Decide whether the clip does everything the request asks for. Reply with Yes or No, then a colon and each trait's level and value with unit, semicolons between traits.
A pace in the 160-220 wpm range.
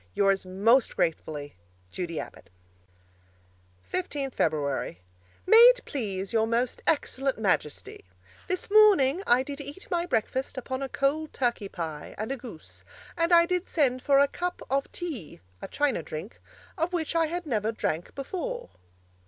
No: average, 150 wpm